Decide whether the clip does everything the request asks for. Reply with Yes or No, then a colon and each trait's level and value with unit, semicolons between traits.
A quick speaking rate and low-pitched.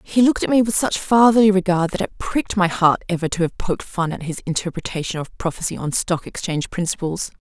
No: fast, 220 wpm; medium, 180 Hz